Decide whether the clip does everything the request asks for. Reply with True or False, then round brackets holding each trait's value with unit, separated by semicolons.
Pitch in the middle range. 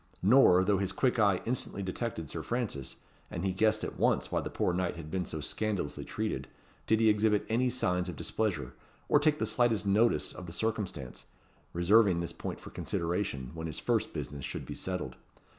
False (100 Hz)